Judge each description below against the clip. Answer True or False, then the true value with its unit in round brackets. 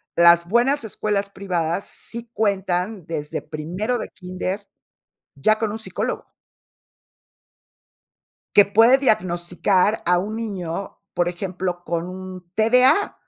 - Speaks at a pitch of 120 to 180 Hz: False (190 Hz)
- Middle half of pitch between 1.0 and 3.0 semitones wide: False (3.7 semitones)